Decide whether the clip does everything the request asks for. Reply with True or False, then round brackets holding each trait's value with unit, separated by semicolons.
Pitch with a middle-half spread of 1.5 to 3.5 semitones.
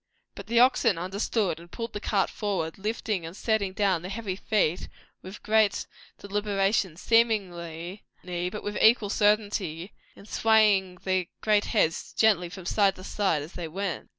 True (2.9 semitones)